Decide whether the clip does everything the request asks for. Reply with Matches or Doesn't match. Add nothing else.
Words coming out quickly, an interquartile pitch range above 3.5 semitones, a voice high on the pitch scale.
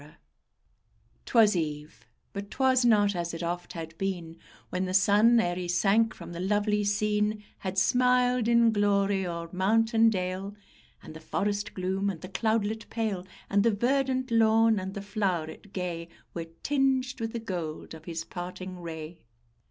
Doesn't match